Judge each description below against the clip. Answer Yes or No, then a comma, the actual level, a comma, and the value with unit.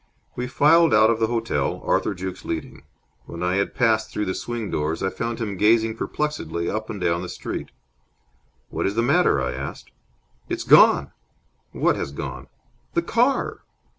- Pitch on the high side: No, low, 110 Hz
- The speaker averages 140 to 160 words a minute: No, average, 170 wpm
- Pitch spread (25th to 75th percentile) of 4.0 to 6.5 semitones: Yes, average, 4.5 semitones